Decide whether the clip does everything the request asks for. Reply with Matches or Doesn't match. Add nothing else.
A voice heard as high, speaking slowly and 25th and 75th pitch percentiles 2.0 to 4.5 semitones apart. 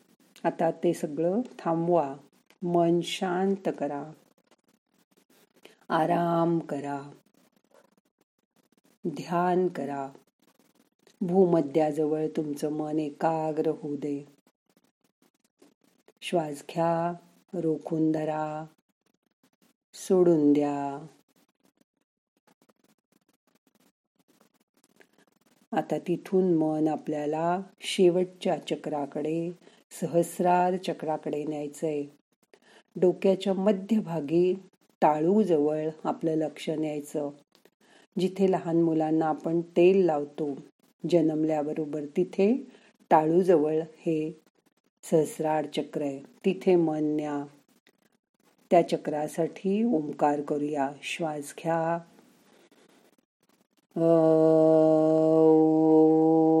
Doesn't match